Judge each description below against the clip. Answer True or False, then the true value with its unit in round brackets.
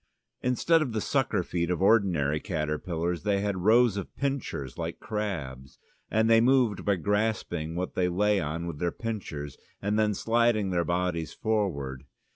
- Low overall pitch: True (95 Hz)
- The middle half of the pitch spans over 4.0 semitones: True (4.8 semitones)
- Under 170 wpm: True (160 wpm)